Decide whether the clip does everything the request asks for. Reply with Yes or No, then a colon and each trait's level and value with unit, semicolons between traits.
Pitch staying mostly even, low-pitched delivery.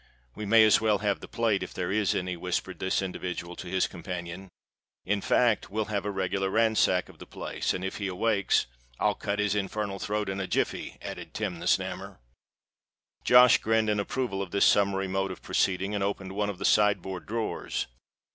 Yes: narrow, 2.0 semitones; low, 100 Hz